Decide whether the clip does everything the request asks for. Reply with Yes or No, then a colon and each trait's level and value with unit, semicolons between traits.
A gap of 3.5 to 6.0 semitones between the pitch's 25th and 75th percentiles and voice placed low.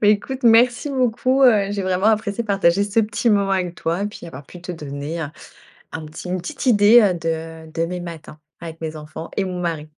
No: average, 4.6 semitones; medium, 185 Hz